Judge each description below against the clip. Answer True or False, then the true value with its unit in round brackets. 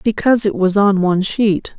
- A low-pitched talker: False (200 Hz)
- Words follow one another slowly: False (200 wpm)